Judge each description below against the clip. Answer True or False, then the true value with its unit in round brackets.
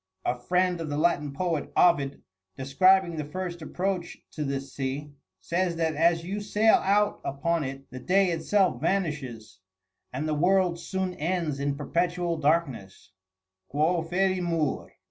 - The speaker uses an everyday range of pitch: True (4.1 semitones)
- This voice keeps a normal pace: True (145 wpm)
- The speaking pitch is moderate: True (165 Hz)